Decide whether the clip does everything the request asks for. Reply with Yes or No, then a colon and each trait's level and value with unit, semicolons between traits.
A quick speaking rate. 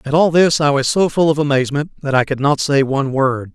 Yes: fast, 270 wpm